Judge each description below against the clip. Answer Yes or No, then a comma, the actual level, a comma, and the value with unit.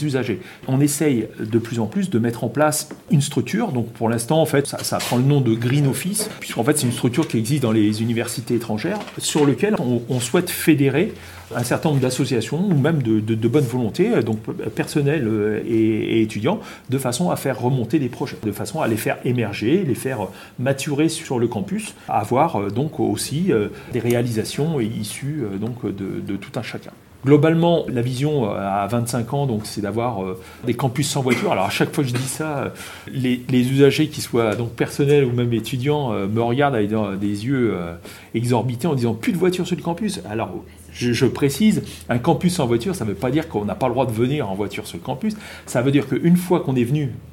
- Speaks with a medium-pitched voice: No, low, 125 Hz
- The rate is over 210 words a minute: Yes, fast, 220 wpm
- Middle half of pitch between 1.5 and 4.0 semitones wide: No, average, 4.8 semitones